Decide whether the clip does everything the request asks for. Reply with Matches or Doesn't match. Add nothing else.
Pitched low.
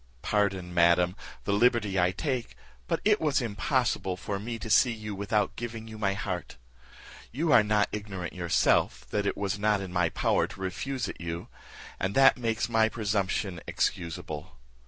Matches